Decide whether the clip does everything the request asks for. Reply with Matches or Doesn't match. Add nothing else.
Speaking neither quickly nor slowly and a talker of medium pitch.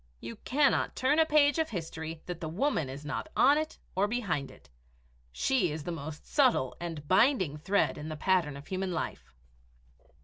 Matches